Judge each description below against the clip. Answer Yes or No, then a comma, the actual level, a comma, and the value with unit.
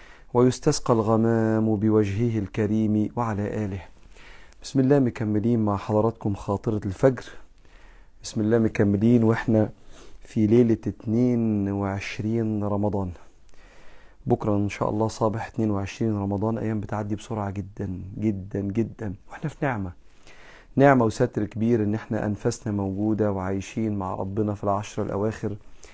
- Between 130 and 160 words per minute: No, average, 115 wpm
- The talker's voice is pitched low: Yes, low, 105 Hz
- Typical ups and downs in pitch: No, narrow, 2.2 semitones